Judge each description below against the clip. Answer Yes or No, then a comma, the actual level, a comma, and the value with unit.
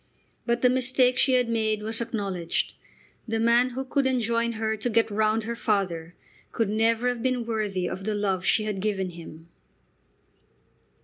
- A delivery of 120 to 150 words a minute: No, average, 170 wpm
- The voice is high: Yes, high, 225 Hz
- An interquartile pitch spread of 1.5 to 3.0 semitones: Yes, narrow, 2.6 semitones